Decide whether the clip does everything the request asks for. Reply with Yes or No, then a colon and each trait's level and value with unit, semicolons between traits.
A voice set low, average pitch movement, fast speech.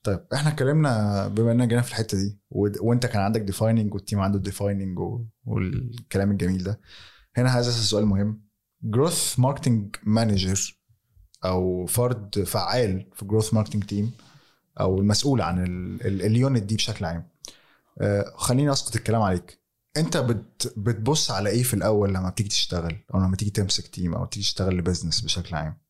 Yes: low, 105 Hz; average, 3.8 semitones; fast, 150 wpm